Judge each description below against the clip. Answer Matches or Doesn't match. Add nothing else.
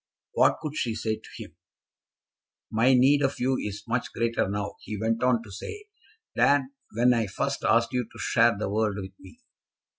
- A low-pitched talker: Matches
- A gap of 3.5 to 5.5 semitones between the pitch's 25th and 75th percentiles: Doesn't match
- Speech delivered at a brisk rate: Doesn't match